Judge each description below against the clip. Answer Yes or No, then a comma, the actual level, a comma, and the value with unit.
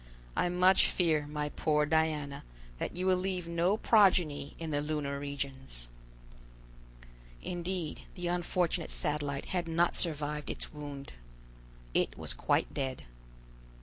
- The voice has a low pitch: No, medium, 155 Hz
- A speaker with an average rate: No, slow, 125 wpm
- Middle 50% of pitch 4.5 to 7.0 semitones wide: No, average, 3.4 semitones